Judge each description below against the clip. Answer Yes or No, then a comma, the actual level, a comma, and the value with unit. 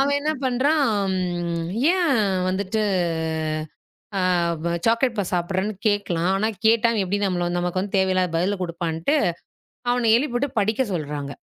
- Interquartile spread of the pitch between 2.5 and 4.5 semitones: No, average, 5.1 semitones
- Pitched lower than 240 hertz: Yes, high, 200 Hz